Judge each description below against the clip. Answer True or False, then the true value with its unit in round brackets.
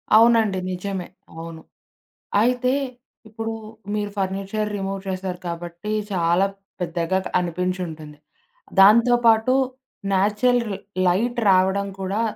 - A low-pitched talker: False (195 Hz)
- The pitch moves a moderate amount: True (3.5 semitones)